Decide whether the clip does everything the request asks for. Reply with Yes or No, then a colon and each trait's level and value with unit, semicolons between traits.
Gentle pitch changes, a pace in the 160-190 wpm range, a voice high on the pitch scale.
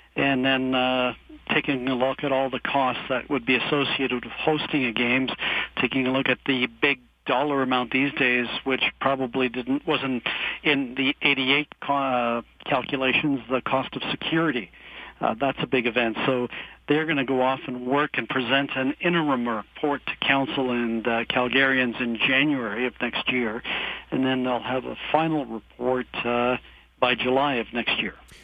No: narrow, 1.9 semitones; average, 175 wpm; low, 130 Hz